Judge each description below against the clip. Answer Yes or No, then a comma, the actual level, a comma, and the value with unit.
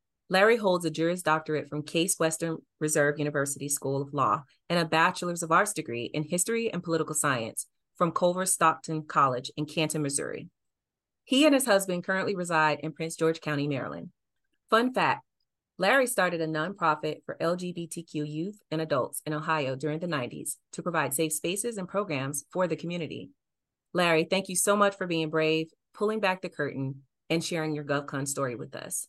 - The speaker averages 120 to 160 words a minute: No, average, 175 wpm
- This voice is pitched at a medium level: Yes, medium, 160 Hz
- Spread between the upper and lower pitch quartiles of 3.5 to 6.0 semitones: No, average, 3.1 semitones